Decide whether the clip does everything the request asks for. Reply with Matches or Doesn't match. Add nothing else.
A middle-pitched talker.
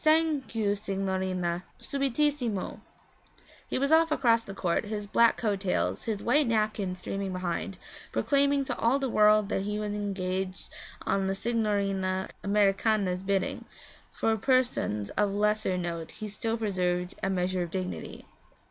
Doesn't match